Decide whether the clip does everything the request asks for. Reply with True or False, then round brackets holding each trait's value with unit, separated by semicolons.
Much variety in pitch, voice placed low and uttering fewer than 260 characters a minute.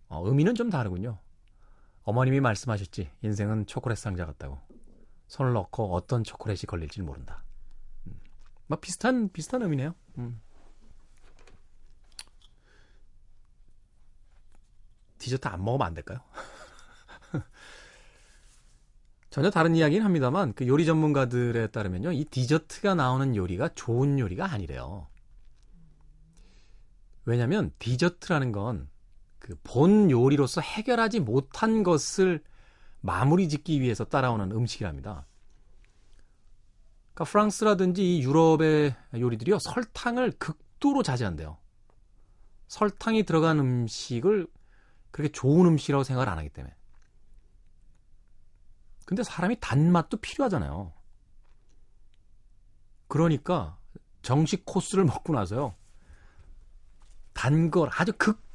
True (9.0 semitones; 120 Hz; 250 characters per minute)